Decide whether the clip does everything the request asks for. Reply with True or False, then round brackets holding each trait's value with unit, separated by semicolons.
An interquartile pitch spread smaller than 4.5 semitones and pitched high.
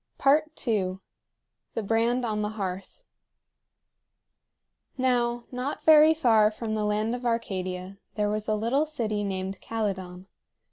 True (3.5 semitones; 220 Hz)